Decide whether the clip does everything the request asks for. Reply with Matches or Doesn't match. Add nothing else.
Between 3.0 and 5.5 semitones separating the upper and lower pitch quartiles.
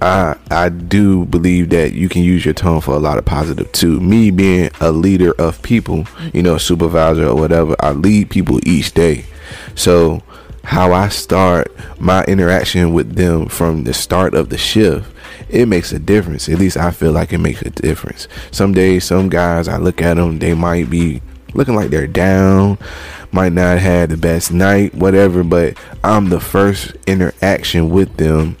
Doesn't match